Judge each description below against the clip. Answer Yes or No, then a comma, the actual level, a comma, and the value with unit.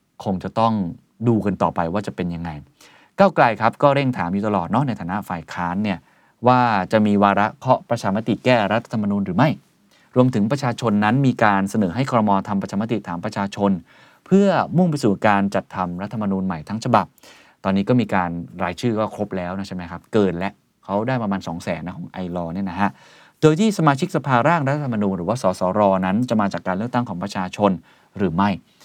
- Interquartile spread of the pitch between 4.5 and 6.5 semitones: No, average, 4.0 semitones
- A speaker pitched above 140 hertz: No, low, 100 Hz